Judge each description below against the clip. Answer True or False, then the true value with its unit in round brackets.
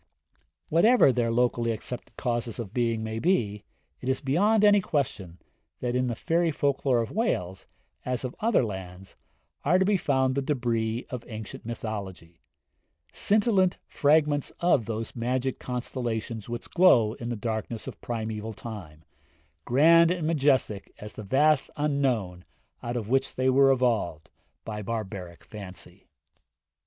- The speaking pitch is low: True (120 Hz)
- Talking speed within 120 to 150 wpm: True (145 wpm)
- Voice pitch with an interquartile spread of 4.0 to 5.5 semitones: True (4.5 semitones)